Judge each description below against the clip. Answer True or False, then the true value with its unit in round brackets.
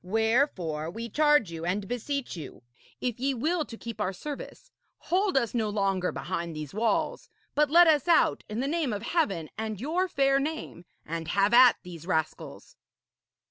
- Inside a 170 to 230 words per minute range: True (175 wpm)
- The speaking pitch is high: True (230 Hz)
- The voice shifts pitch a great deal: True (7.9 semitones)